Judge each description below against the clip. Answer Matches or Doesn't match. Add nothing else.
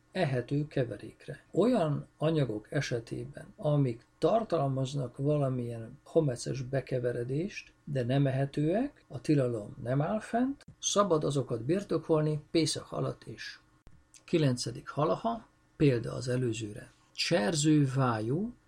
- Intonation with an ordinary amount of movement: Matches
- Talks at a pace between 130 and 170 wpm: Doesn't match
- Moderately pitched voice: Matches